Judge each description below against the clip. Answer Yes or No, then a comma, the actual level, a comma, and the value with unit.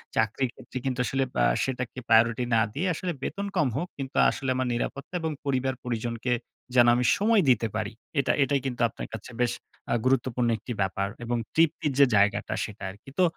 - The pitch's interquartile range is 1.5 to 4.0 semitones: Yes, average, 2.9 semitones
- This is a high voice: No, low, 125 Hz